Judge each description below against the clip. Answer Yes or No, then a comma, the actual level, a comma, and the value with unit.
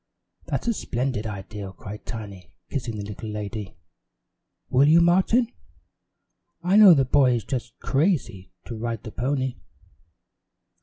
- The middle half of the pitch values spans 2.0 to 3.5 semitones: No, wide, 5.5 semitones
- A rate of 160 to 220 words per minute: No, slow, 135 wpm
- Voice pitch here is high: No, low, 120 Hz